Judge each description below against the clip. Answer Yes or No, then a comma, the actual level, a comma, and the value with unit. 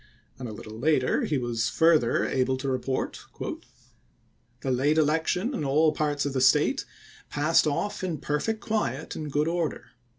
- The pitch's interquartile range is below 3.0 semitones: No, average, 3.5 semitones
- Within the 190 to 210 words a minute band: No, average, 175 wpm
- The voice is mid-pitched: Yes, medium, 145 Hz